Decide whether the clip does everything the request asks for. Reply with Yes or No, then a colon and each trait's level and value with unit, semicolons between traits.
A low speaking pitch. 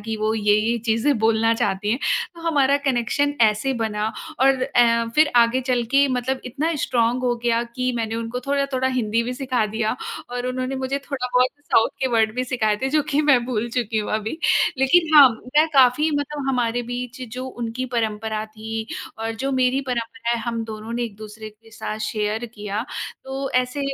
No: high, 245 Hz